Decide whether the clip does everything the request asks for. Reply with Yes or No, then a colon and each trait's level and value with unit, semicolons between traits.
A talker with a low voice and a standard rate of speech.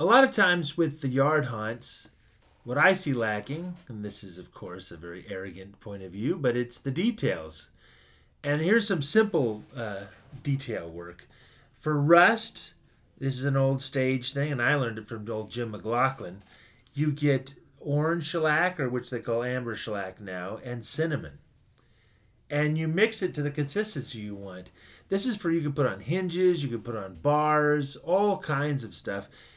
Yes: low, 130 Hz; average, 180 wpm